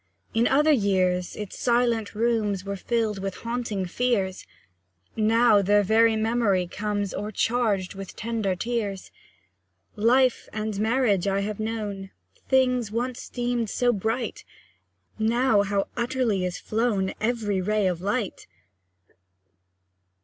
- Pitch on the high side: Yes, high, 215 Hz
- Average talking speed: No, slow, 120 wpm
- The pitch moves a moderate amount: Yes, average, 3.2 semitones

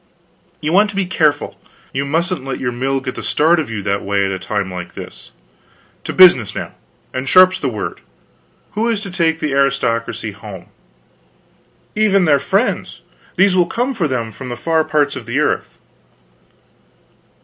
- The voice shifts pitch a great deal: Yes, wide, 7.0 semitones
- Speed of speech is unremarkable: Yes, average, 175 wpm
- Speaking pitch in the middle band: Yes, medium, 145 Hz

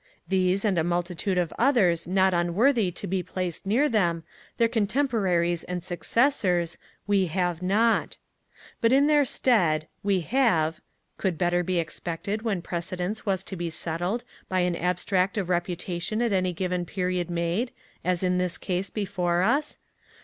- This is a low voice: No, medium, 185 Hz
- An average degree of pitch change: Yes, average, 3.0 semitones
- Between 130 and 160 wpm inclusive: Yes, average, 155 wpm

